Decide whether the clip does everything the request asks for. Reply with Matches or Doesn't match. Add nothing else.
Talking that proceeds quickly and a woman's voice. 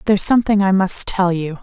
Matches